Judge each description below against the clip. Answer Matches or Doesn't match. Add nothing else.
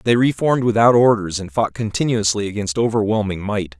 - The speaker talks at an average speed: Matches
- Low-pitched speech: Matches